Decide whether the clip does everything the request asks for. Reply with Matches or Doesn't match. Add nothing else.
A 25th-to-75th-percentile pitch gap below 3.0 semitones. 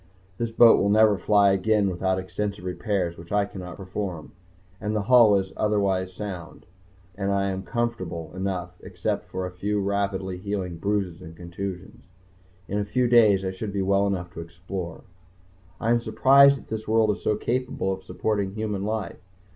Matches